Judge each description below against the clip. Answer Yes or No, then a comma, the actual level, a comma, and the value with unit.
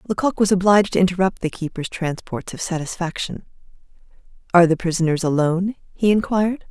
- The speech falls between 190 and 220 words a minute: No, average, 145 wpm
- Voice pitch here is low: No, medium, 180 Hz